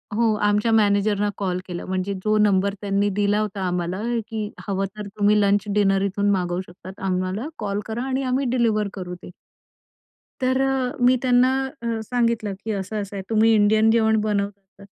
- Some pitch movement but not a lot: No, narrow, 2.2 semitones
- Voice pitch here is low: No, high, 205 Hz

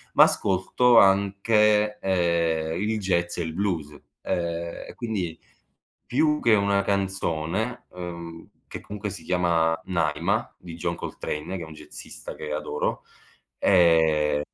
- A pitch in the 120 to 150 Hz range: No, very low, 90 Hz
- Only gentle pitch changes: No, average, 3.5 semitones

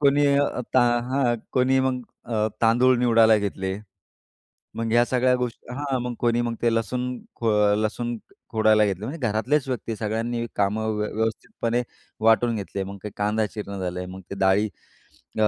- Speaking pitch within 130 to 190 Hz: No, low, 115 Hz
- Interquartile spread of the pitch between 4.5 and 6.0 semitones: No, average, 2.8 semitones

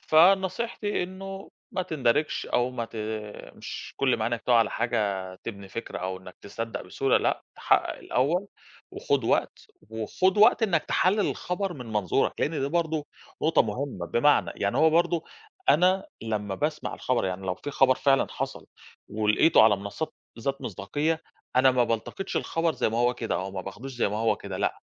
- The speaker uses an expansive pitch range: Yes, wide, 7.0 semitones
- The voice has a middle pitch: No, low, 130 Hz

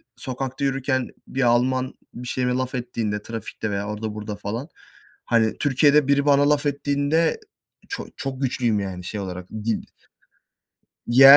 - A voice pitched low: Yes, low, 125 Hz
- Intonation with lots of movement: No, average, 4.1 semitones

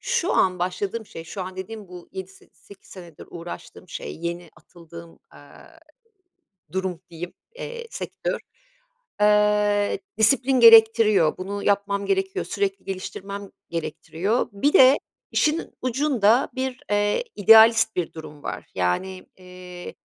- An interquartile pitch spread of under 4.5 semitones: Yes, average, 4.1 semitones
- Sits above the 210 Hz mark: No, high, 200 Hz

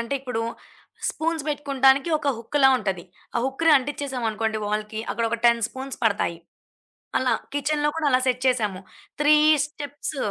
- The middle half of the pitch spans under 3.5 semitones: No, average, 4.3 semitones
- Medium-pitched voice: No, very high, 260 Hz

